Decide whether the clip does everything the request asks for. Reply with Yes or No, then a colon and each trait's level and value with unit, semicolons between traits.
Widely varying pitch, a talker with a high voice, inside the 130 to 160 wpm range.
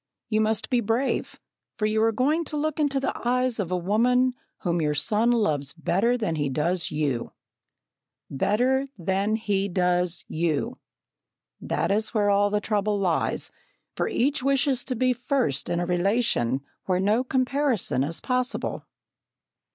Yes: wide, 6.2 semitones; high, 210 Hz; average, 155 wpm